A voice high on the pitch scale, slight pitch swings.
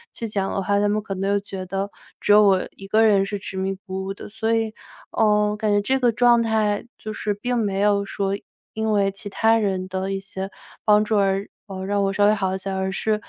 Yes: high, 205 Hz; narrow, 1.7 semitones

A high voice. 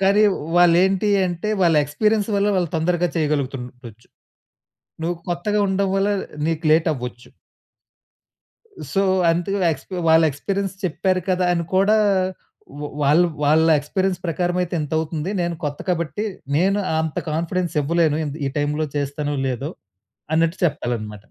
No: medium, 165 Hz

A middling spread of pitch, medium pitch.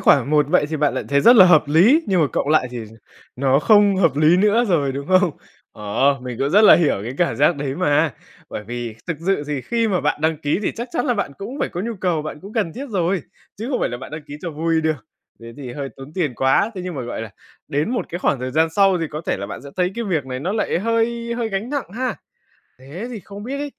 No: wide, 6.5 semitones; medium, 165 Hz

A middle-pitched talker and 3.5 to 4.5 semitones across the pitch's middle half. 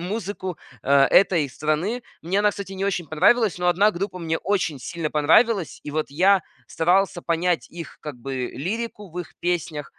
Yes: medium, 175 Hz; average, 4.2 semitones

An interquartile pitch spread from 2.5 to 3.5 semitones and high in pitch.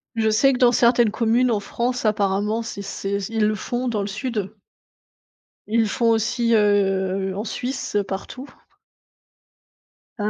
Yes: average, 2.8 semitones; high, 220 Hz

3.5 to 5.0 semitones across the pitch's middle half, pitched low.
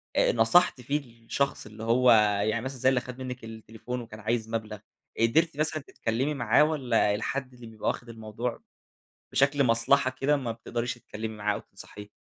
No: average, 2.9 semitones; low, 120 Hz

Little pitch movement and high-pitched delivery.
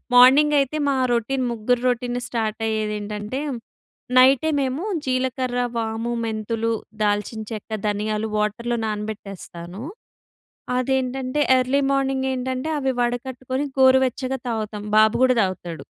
No: average, 3.3 semitones; high, 240 Hz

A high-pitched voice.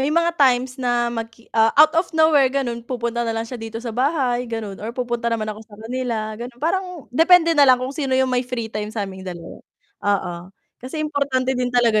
Yes: high, 245 Hz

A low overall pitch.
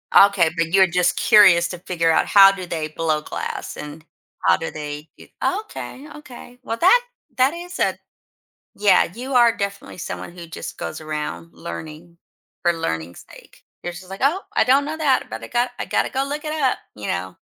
No: medium, 185 Hz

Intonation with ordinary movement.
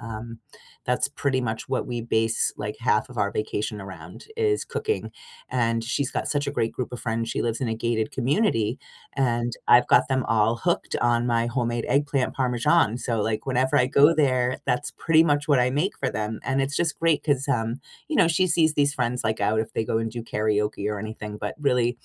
Yes: average, 3.7 semitones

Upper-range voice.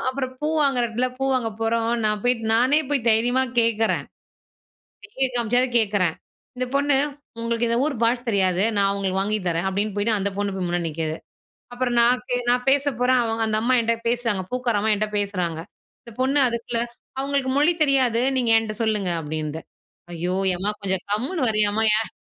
Yes: high, 230 Hz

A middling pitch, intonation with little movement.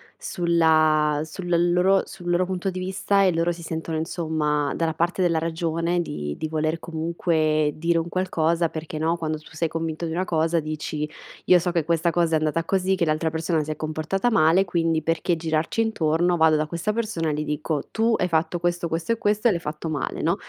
Yes: medium, 165 Hz; narrow, 1.9 semitones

